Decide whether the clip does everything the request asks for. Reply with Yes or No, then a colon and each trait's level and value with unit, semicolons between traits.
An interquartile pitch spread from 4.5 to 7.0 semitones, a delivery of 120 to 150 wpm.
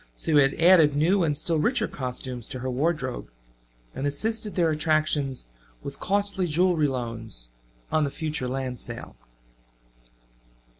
Yes: average, 4.8 semitones; average, 140 wpm